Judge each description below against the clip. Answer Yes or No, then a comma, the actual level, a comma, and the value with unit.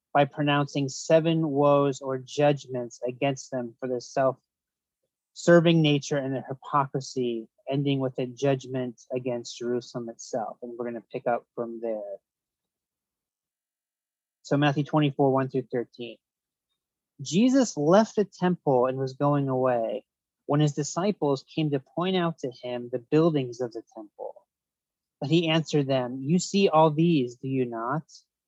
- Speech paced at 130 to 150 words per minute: Yes, average, 145 wpm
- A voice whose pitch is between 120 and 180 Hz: Yes, low, 135 Hz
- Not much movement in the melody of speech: No, average, 3.4 semitones